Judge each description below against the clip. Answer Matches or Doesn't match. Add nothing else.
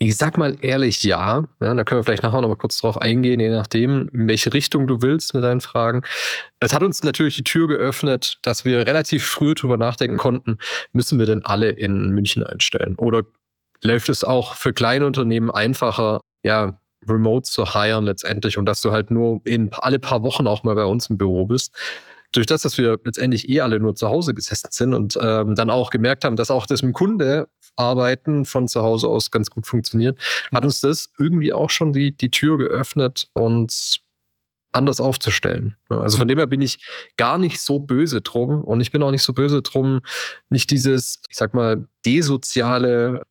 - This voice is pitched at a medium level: Doesn't match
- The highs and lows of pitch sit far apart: Doesn't match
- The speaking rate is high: Matches